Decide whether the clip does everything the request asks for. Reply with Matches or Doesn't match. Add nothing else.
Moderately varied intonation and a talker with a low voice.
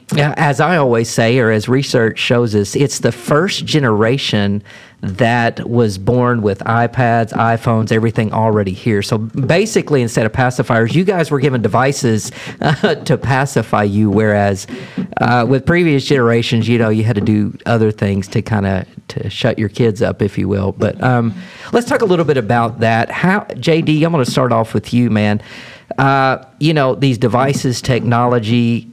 Matches